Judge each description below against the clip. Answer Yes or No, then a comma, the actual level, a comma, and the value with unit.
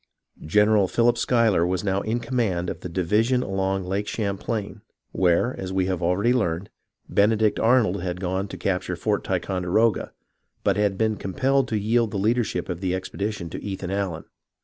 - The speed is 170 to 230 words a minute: Yes, average, 180 wpm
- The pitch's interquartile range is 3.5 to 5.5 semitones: No, average, 3.1 semitones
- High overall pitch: No, low, 100 Hz